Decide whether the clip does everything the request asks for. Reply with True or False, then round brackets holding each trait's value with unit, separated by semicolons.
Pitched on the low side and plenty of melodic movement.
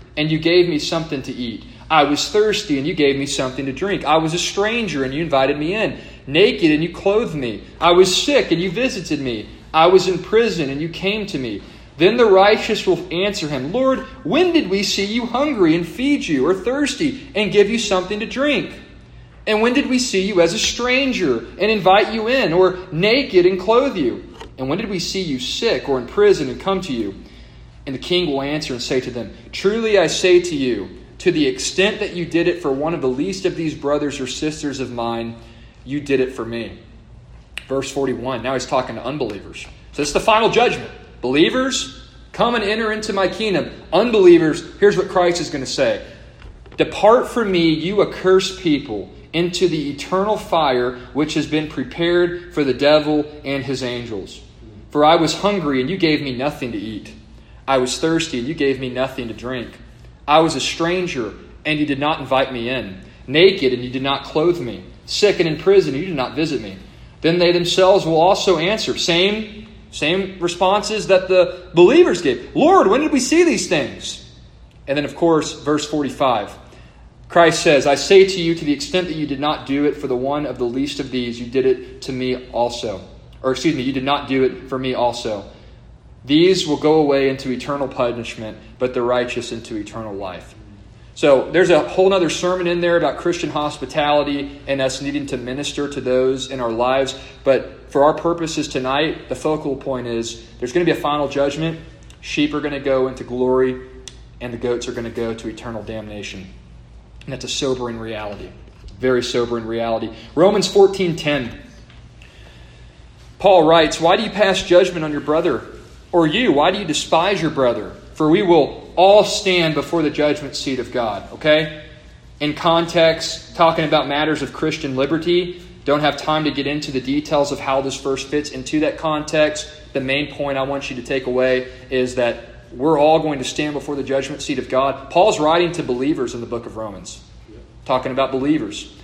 False (150 Hz; 5.8 semitones)